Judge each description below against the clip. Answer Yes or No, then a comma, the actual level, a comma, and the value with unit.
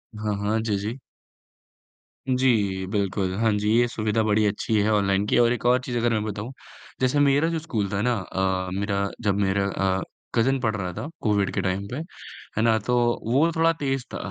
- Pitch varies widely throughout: No, average, 3.5 semitones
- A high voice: No, low, 110 Hz